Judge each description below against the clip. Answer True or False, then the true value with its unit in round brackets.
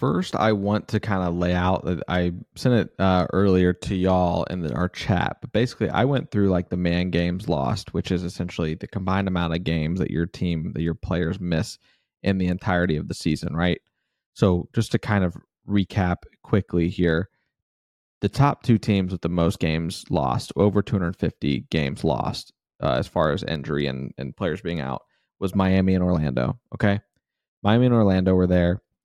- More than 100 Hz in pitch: False (90 Hz)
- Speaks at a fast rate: False (190 wpm)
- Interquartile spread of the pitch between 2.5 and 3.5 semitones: True (2.9 semitones)